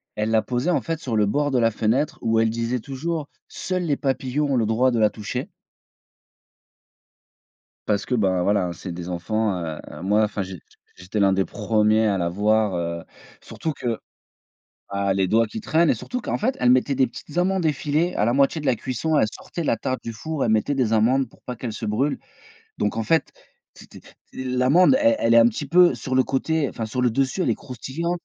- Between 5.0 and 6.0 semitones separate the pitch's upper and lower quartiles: Yes, average, 5.3 semitones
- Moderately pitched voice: No, low, 120 Hz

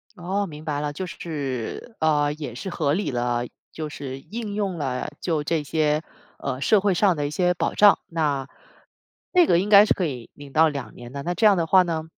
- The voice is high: No, medium, 155 Hz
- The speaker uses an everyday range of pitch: Yes, average, 4.5 semitones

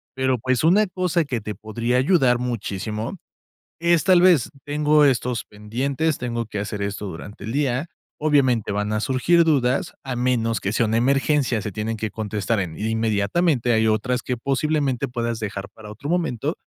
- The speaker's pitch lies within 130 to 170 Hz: No, low, 120 Hz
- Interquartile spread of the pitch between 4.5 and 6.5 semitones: Yes, average, 4.9 semitones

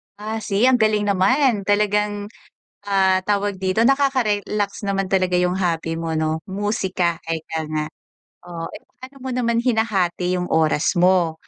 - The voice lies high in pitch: Yes, high, 195 Hz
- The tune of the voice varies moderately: Yes, average, 3.1 semitones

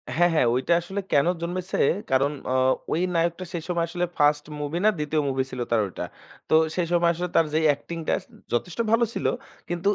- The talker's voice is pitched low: No, medium, 165 Hz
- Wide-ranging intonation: No, average, 3.0 semitones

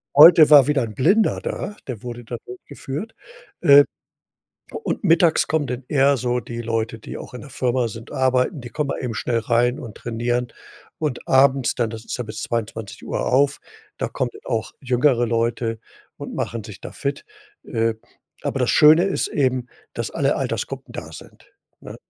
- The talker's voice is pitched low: Yes, low, 125 Hz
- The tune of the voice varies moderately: Yes, average, 3.3 semitones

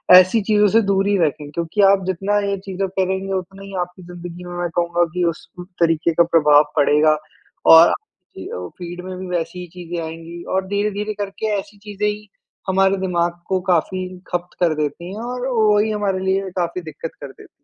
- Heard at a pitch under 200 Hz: Yes, medium, 185 Hz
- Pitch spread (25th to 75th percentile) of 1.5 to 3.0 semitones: Yes, narrow, 2.5 semitones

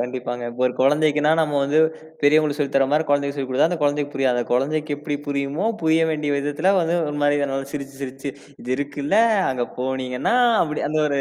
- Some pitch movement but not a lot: No, narrow, 1.9 semitones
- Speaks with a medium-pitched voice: Yes, medium, 145 Hz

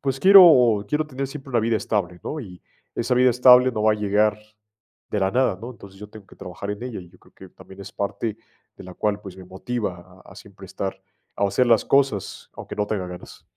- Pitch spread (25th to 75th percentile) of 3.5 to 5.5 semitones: Yes, average, 4.5 semitones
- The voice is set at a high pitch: No, low, 105 Hz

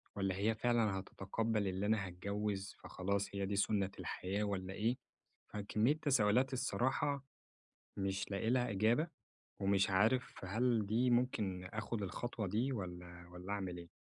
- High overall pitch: No, low, 105 Hz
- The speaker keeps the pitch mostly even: No, average, 3.1 semitones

